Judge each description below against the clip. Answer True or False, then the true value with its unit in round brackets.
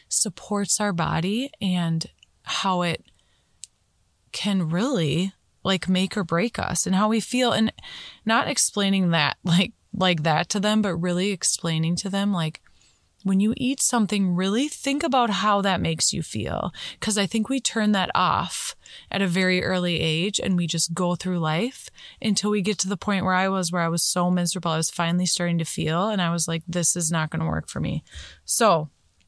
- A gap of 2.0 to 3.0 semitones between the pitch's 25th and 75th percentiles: False (3.7 semitones)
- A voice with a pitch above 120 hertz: True (185 Hz)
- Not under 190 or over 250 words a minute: True (195 wpm)